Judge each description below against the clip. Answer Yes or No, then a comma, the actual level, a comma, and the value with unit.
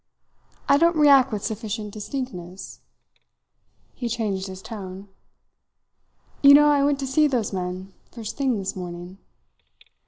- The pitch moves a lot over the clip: Yes, wide, 6.3 semitones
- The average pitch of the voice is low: No, high, 220 Hz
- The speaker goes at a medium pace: No, slow, 130 wpm